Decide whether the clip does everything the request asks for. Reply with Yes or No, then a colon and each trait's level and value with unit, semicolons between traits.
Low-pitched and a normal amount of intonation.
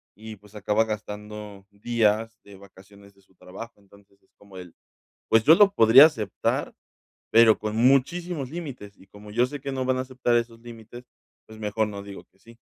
Yes: low, 110 Hz; average, 3.1 semitones